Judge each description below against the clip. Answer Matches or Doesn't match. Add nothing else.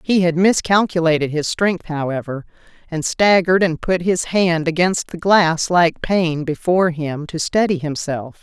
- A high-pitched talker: Doesn't match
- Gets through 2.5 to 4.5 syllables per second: Matches